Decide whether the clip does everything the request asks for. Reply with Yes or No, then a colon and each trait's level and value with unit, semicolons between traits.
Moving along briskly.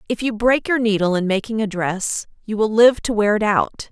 Yes: fast, 245 wpm